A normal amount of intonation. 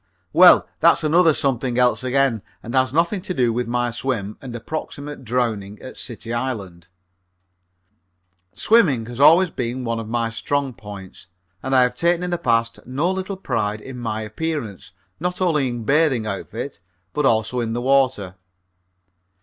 Yes: average, 4.3 semitones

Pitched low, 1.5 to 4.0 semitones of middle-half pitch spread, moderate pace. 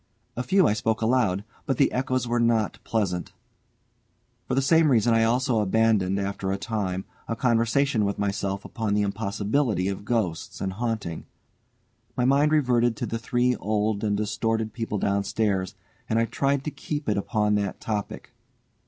Yes: low, 110 Hz; average, 3.3 semitones; average, 165 wpm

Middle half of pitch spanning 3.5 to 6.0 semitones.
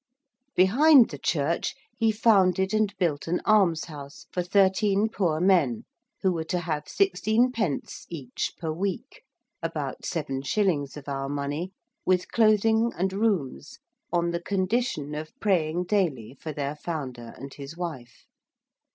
Yes: wide, 5.4 semitones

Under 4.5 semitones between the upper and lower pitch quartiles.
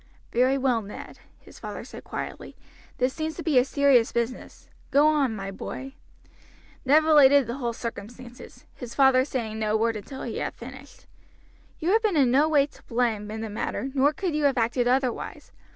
Yes: average, 3.3 semitones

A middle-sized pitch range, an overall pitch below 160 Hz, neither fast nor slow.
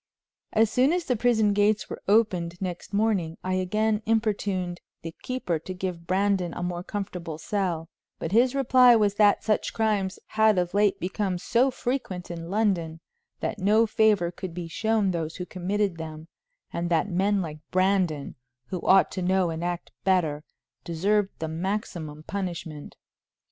No: average, 3.5 semitones; high, 190 Hz; average, 160 wpm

